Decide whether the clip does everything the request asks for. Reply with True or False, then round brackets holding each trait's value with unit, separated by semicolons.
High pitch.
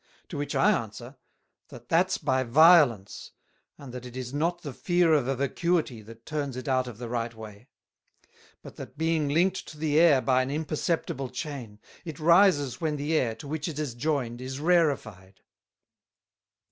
False (140 Hz)